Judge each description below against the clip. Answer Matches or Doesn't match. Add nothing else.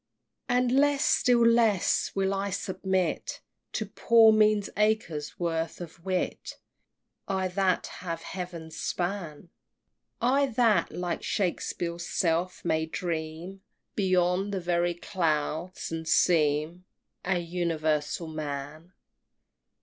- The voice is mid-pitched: Matches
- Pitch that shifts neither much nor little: Matches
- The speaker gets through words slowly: Matches